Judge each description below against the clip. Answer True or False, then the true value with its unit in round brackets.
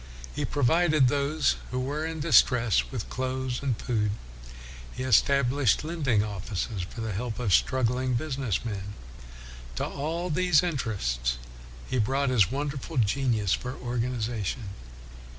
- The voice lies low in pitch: True (125 Hz)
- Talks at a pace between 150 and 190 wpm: False (135 wpm)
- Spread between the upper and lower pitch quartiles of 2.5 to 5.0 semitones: True (4.5 semitones)